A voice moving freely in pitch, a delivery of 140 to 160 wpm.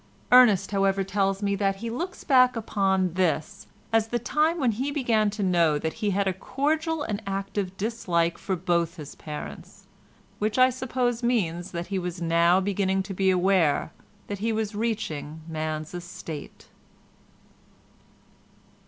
No: average, 4.5 semitones; average, 155 wpm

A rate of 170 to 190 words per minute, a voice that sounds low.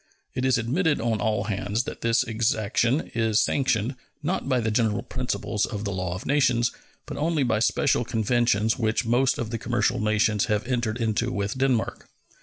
Yes: average, 180 wpm; low, 115 Hz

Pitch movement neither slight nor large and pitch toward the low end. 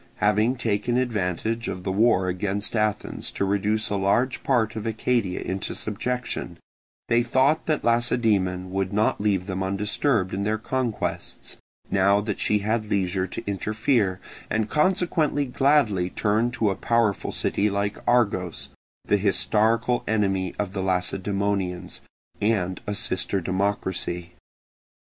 Yes: average, 3.4 semitones; low, 105 Hz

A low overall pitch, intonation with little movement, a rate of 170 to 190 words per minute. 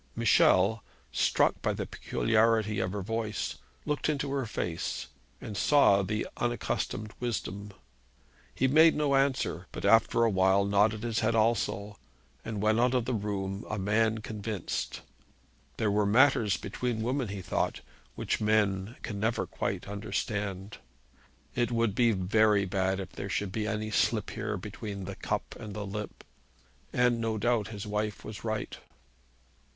No: low, 110 Hz; narrow, 2.3 semitones; average, 155 wpm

